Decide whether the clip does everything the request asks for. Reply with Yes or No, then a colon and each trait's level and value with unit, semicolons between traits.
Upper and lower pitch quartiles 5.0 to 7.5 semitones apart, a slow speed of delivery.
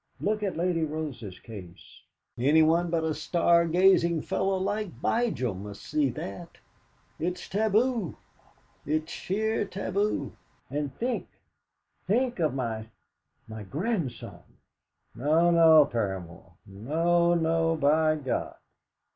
Yes: wide, 5.5 semitones; slow, 110 wpm